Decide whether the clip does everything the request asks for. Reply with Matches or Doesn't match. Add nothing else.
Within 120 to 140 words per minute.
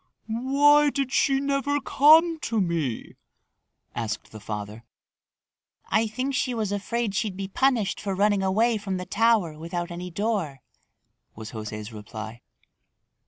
Matches